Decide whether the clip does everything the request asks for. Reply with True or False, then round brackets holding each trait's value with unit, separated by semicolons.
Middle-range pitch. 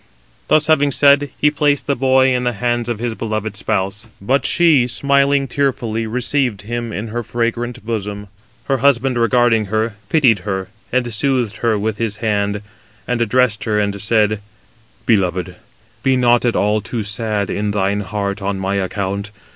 False (115 Hz)